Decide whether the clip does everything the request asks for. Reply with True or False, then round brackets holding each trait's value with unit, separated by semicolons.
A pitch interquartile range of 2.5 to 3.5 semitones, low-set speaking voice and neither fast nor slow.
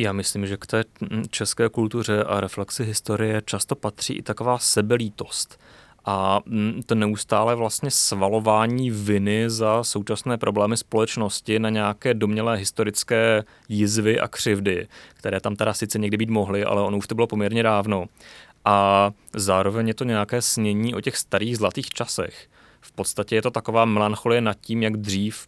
False (1.8 semitones; 110 Hz; 160 wpm)